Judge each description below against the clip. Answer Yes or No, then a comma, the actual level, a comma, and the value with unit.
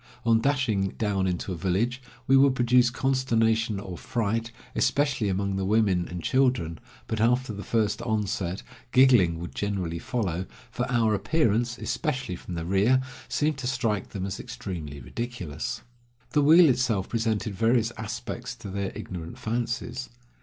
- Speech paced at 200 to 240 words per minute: No, average, 150 wpm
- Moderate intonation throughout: Yes, average, 4.5 semitones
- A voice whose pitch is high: No, low, 110 Hz